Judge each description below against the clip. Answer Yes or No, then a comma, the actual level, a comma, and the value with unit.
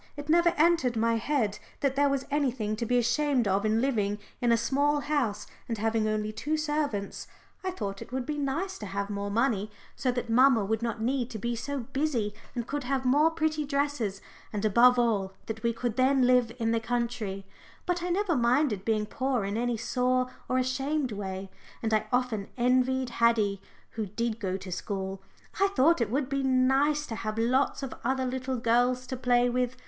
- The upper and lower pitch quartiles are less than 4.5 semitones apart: Yes, average, 3.8 semitones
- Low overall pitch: No, high, 245 Hz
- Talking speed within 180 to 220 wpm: Yes, average, 200 wpm